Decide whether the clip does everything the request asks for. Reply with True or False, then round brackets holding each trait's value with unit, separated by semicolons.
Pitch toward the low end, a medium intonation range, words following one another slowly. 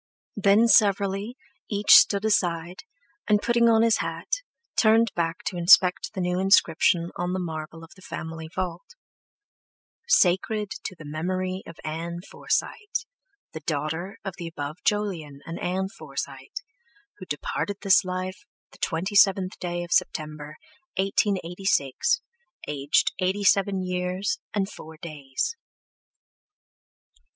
False (185 Hz; 3.5 semitones; 125 wpm)